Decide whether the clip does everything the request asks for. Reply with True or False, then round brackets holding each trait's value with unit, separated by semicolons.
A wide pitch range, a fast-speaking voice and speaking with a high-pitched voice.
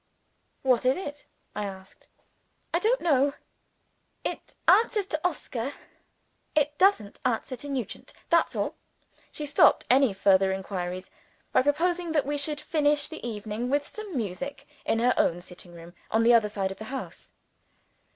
False (6.3 semitones; 155 wpm; 260 Hz)